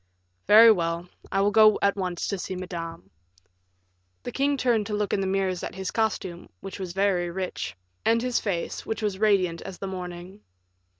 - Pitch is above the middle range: Yes, high, 195 Hz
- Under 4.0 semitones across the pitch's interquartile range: Yes, average, 2.9 semitones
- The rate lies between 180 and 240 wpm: Yes, average, 185 wpm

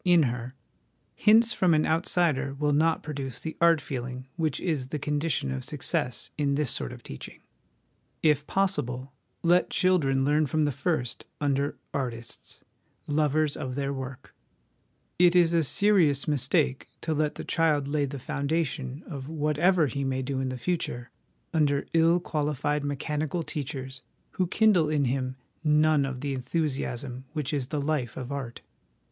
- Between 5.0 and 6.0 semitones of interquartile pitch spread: No, average, 3.2 semitones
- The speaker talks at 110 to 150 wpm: No, average, 160 wpm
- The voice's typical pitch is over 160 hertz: No, medium, 145 Hz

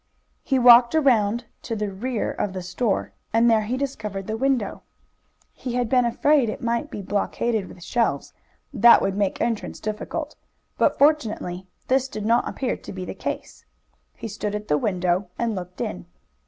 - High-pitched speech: Yes, high, 220 Hz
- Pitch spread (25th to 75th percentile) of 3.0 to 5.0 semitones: Yes, average, 3.7 semitones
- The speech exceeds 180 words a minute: No, average, 175 wpm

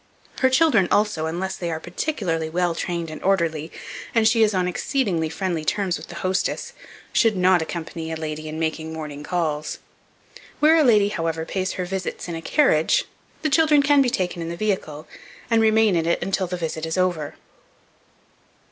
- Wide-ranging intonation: No, average, 4.7 semitones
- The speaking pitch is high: No, medium, 180 Hz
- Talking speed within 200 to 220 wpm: No, average, 185 wpm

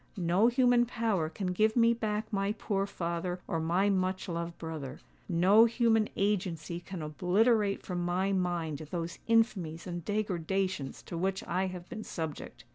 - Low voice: No, medium, 185 Hz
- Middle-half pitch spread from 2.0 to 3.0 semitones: No, average, 3.8 semitones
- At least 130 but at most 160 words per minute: Yes, average, 155 wpm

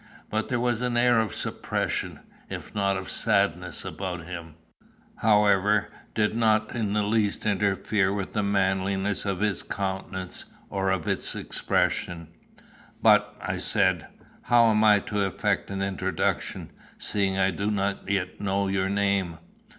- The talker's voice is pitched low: Yes, low, 100 Hz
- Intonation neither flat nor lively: No, narrow, 1.8 semitones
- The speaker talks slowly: No, average, 145 wpm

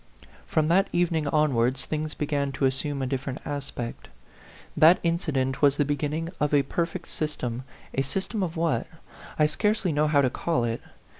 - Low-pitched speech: No, medium, 150 Hz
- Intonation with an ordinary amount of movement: Yes, average, 3.4 semitones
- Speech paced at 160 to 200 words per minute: Yes, average, 170 wpm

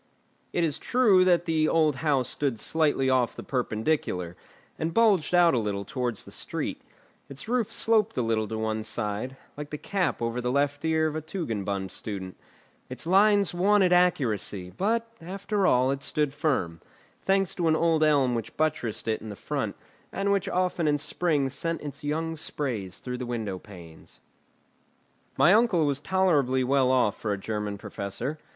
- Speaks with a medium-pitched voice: Yes, medium, 145 Hz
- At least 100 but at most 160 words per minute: No, average, 170 wpm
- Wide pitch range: Yes, wide, 7.1 semitones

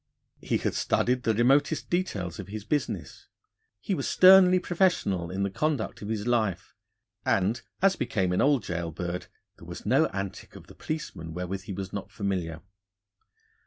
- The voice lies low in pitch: Yes, low, 105 Hz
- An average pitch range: No, wide, 7.7 semitones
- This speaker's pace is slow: No, average, 165 wpm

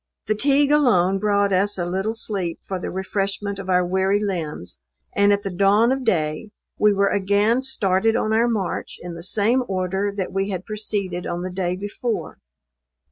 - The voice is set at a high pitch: Yes, high, 200 Hz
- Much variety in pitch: No, narrow, 2.4 semitones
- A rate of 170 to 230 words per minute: Yes, average, 180 wpm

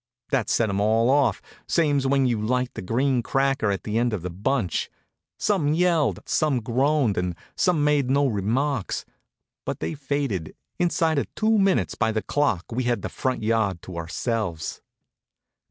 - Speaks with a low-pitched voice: Yes, low, 125 Hz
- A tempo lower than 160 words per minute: No, average, 170 wpm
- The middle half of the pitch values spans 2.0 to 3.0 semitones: No, average, 5.2 semitones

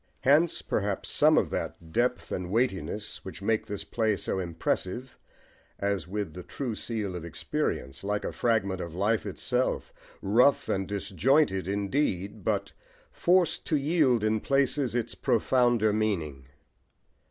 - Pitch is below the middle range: Yes, low, 105 Hz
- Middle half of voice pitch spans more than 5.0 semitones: No, average, 4.4 semitones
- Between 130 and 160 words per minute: Yes, average, 140 wpm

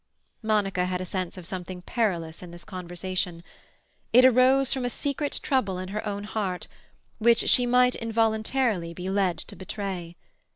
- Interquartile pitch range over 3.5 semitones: Yes, average, 4.5 semitones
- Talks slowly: No, average, 160 wpm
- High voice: Yes, high, 195 Hz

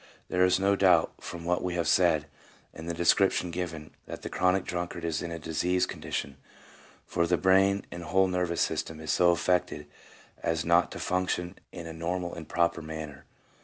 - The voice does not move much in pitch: Yes, narrow, 1.7 semitones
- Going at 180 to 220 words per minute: Yes, average, 185 wpm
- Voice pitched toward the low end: Yes, very low, 85 Hz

